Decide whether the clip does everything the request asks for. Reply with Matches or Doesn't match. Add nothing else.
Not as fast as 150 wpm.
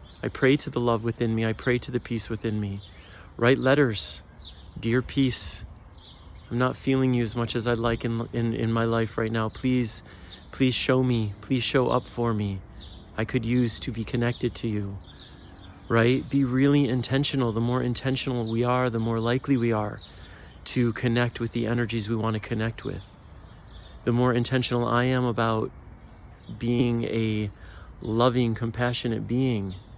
Doesn't match